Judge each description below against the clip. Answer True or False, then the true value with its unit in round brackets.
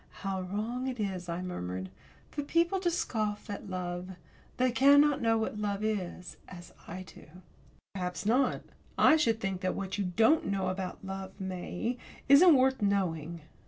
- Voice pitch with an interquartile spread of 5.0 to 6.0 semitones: True (5.4 semitones)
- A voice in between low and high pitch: False (200 Hz)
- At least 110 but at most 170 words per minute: True (160 wpm)